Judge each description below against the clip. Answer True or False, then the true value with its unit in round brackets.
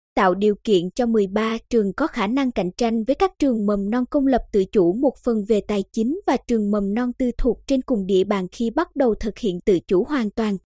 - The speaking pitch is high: True (225 Hz)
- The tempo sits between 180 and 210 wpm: False (245 wpm)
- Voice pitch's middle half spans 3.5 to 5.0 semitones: True (3.8 semitones)